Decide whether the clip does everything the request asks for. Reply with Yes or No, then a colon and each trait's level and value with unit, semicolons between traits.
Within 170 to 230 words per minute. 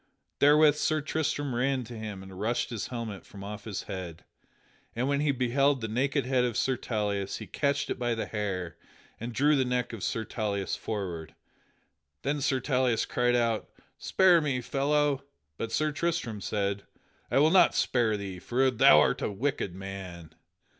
Yes: average, 175 wpm